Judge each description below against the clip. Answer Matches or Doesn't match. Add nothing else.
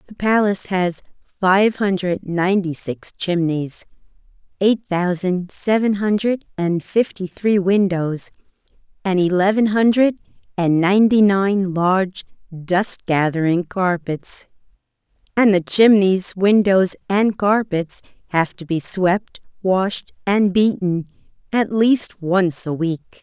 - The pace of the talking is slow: Matches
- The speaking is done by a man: Doesn't match